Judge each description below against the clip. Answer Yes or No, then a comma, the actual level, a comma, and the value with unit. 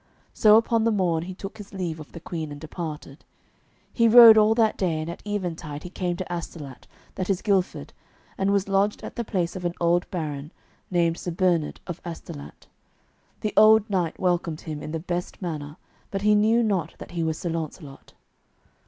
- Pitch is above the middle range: No, medium, 175 Hz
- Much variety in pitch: No, average, 3.8 semitones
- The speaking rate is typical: Yes, average, 195 wpm